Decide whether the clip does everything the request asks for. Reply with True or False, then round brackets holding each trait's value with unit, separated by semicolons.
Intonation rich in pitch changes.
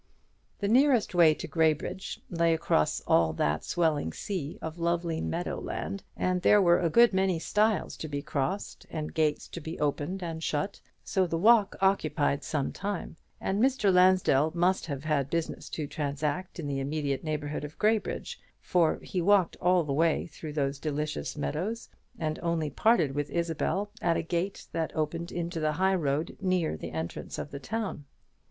False (3.9 semitones)